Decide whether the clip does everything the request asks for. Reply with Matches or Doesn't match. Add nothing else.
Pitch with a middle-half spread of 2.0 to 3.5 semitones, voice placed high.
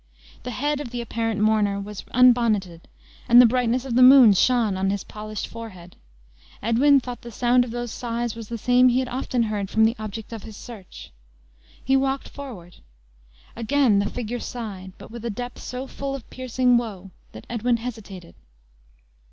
Matches